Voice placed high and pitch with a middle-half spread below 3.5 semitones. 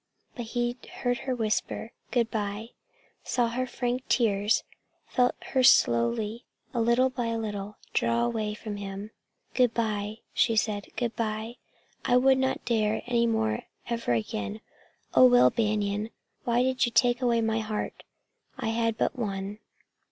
Yes: high, 225 Hz; average, 2.8 semitones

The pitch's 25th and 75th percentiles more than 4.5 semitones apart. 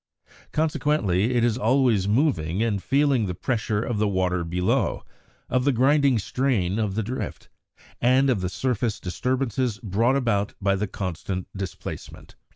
Yes: average, 5.0 semitones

